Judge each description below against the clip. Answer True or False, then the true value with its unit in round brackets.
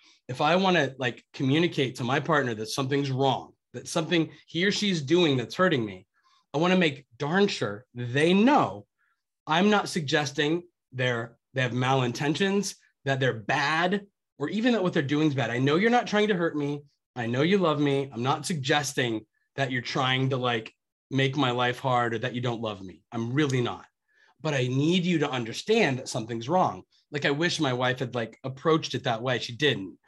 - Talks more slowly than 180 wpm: False (205 wpm)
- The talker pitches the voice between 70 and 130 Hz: False (140 Hz)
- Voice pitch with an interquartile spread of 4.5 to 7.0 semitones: True (5.1 semitones)